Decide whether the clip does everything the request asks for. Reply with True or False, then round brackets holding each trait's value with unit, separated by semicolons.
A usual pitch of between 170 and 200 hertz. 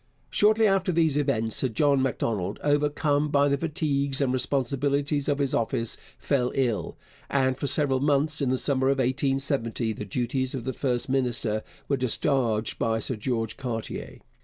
False (135 Hz)